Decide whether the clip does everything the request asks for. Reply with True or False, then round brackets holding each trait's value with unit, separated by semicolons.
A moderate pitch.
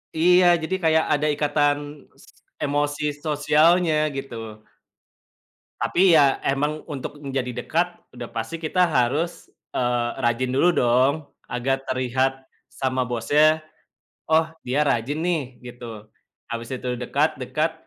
True (145 Hz)